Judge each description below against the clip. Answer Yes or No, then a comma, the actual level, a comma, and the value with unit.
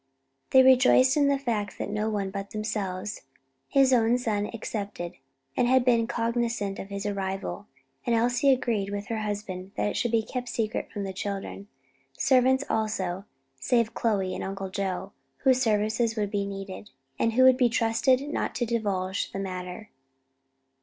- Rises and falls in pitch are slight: No, average, 3.4 semitones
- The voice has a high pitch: Yes, high, 215 Hz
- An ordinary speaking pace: Yes, average, 165 wpm